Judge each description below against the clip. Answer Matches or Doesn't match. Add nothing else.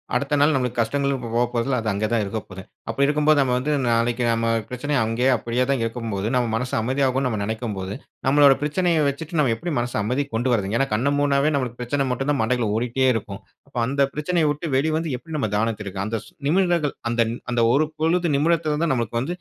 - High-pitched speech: Doesn't match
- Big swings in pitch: Doesn't match